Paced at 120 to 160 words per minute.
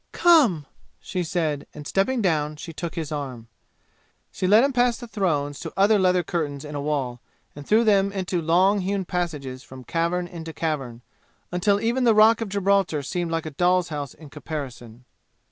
No: average, 180 wpm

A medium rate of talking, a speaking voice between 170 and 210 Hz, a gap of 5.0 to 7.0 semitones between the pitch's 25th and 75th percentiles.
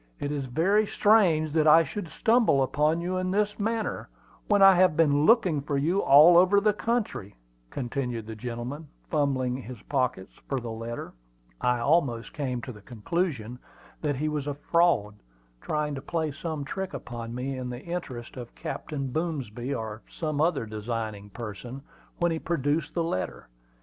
No: average, 170 wpm; medium, 145 Hz; wide, 5.6 semitones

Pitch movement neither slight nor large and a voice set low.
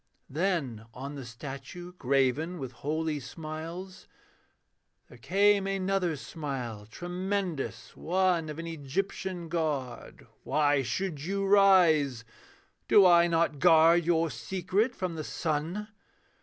No: average, 4.8 semitones; medium, 165 Hz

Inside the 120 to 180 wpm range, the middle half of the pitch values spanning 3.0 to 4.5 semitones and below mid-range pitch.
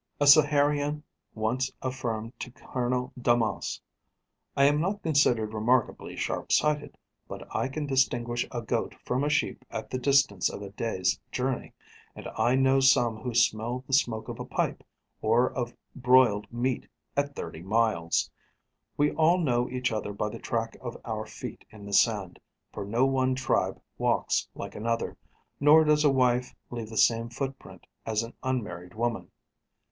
Yes: average, 160 wpm; average, 3.3 semitones; low, 125 Hz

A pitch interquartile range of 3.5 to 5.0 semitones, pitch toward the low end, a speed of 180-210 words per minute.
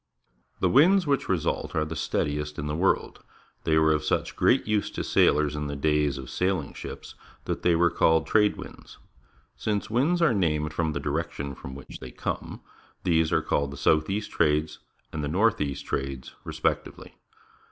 Yes: average, 4.7 semitones; very low, 80 Hz; average, 185 wpm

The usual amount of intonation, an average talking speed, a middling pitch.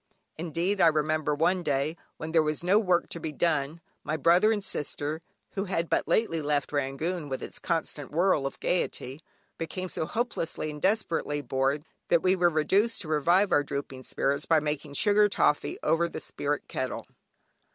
Yes: average, 3.5 semitones; average, 175 wpm; medium, 160 Hz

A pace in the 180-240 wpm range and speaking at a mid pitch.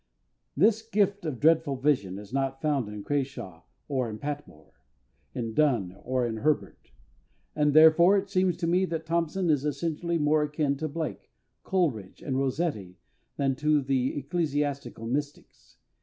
No: average, 150 wpm; medium, 145 Hz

